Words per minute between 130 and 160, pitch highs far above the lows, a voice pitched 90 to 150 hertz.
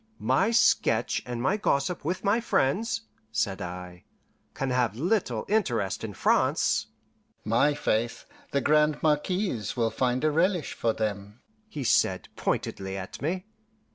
Yes: average, 140 wpm; wide, 8.0 semitones; low, 135 Hz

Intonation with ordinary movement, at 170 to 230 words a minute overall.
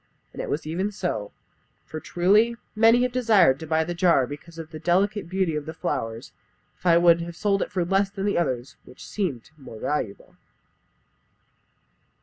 Yes: average, 4.6 semitones; average, 175 wpm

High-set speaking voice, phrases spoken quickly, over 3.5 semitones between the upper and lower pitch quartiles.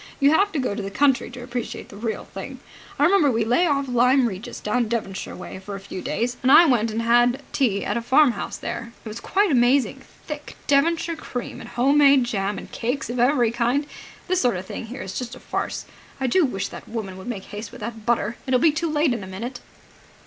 Yes: high, 245 Hz; fast, 235 wpm; average, 4.1 semitones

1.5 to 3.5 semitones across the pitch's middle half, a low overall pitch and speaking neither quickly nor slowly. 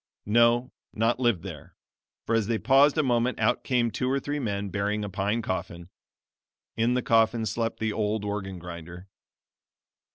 Yes: average, 3.2 semitones; low, 110 Hz; average, 165 wpm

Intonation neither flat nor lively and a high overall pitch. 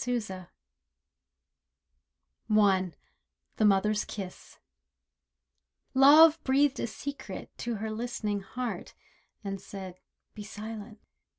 Yes: average, 4.2 semitones; high, 210 Hz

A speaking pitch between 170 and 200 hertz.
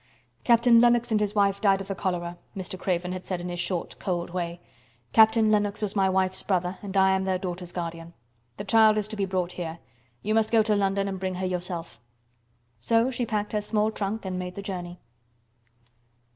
Yes: high, 190 Hz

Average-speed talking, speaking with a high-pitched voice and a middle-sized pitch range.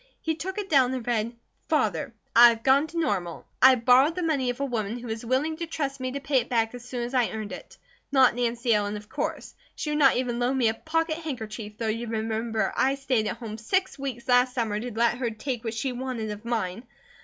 No: fast, 240 wpm; high, 245 Hz; average, 3.4 semitones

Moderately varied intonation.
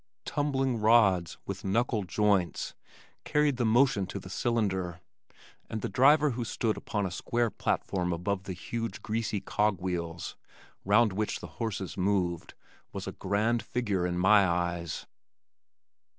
Yes: average, 4.2 semitones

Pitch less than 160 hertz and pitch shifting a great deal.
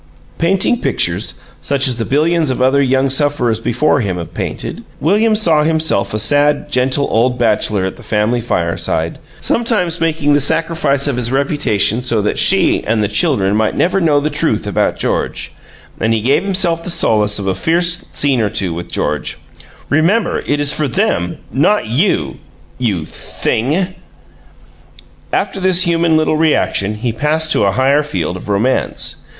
Yes: low, 135 Hz; wide, 6.8 semitones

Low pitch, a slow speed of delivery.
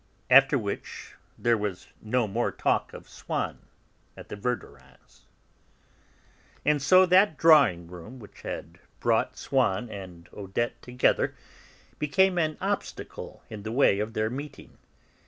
Yes: low, 120 Hz; slow, 130 wpm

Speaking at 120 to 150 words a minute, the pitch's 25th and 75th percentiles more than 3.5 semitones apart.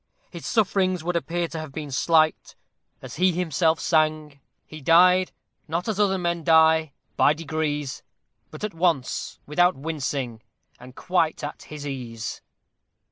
No: slow, 135 wpm; average, 3.2 semitones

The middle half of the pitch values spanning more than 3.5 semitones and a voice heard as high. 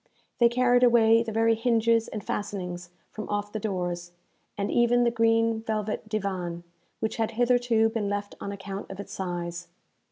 No: narrow, 2.6 semitones; high, 220 Hz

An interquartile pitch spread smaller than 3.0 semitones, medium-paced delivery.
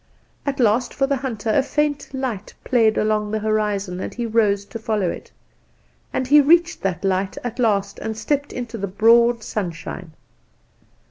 No: average, 4.1 semitones; average, 170 wpm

